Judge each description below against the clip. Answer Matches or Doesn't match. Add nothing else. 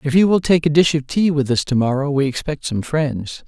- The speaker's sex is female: Doesn't match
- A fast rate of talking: Matches